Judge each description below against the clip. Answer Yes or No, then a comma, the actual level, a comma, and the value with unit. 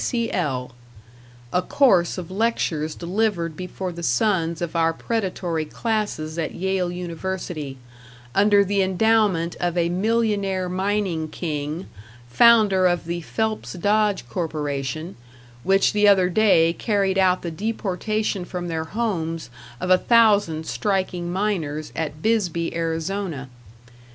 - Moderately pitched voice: Yes, medium, 180 Hz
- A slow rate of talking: Yes, slow, 125 wpm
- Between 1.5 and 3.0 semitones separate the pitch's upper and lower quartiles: No, average, 3.8 semitones